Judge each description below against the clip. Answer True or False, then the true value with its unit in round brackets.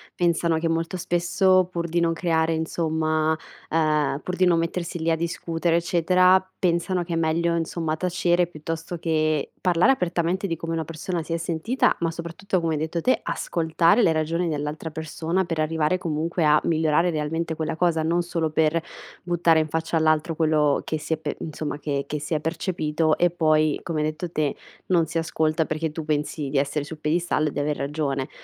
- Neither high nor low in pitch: True (165 Hz)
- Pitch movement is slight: True (1.6 semitones)